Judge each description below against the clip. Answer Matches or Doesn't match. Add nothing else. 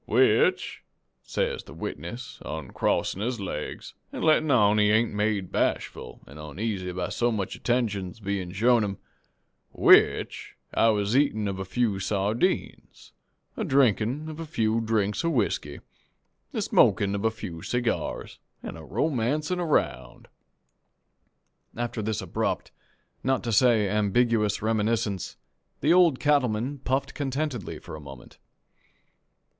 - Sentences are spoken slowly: Matches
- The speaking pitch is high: Doesn't match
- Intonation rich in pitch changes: Doesn't match